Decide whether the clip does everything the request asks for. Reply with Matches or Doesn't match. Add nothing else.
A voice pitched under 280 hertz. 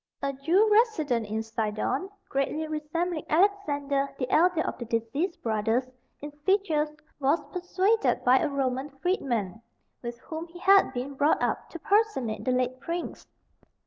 Doesn't match